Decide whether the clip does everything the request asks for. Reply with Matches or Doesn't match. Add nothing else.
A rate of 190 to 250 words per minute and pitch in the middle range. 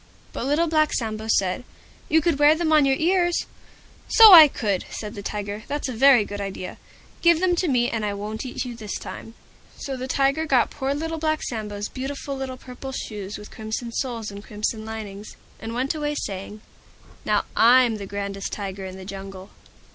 Doesn't match